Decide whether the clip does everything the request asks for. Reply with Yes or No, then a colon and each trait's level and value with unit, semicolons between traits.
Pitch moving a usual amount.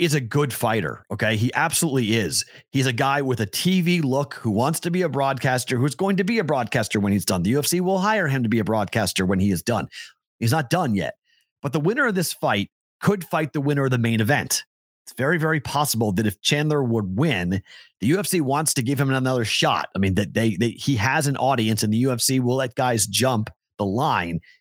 No: wide, 5.7 semitones